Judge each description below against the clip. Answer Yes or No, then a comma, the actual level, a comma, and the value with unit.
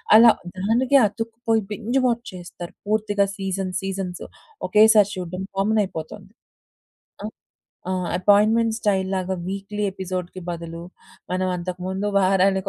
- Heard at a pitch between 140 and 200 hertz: Yes, high, 195 Hz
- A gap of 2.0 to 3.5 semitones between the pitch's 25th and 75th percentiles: Yes, narrow, 2.6 semitones